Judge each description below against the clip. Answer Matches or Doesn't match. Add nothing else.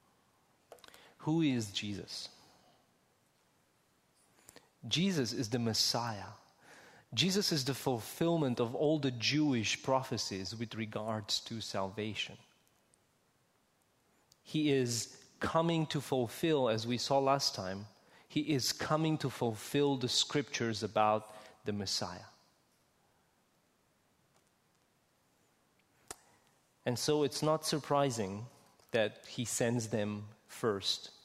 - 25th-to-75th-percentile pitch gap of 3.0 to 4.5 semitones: Doesn't match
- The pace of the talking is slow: Matches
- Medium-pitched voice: Doesn't match